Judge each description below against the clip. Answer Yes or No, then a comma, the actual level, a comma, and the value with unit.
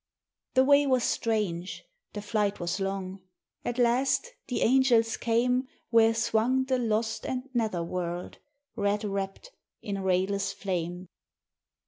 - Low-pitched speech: No, high, 220 Hz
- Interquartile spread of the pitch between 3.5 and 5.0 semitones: Yes, average, 4.3 semitones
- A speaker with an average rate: No, slow, 125 wpm